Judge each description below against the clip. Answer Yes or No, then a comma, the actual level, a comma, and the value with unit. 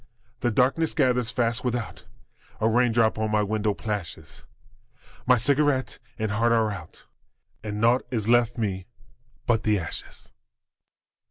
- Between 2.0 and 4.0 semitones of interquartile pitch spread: Yes, narrow, 2.5 semitones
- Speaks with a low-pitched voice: Yes, low, 115 Hz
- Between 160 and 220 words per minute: No, slow, 135 wpm